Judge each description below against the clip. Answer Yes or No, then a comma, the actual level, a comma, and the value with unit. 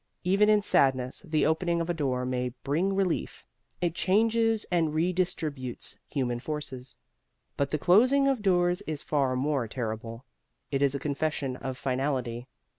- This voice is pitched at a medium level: Yes, medium, 150 Hz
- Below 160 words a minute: Yes, average, 150 wpm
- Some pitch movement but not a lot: No, wide, 5.7 semitones